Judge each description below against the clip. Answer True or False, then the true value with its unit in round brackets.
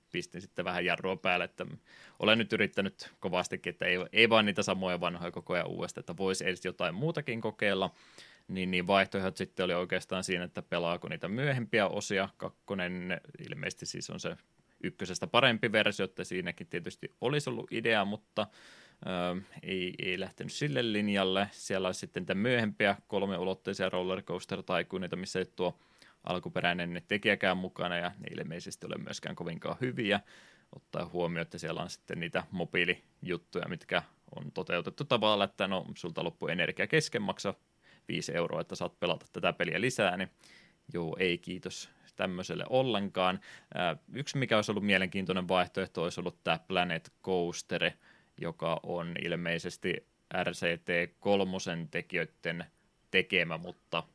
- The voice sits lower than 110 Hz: True (95 Hz)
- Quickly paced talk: False (145 wpm)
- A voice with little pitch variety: True (2.3 semitones)